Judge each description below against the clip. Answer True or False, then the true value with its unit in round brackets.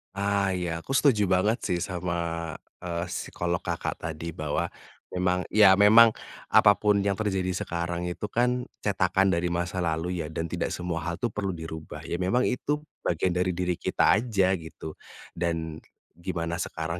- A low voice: True (90 Hz)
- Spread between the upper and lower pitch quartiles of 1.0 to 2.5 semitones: False (2.9 semitones)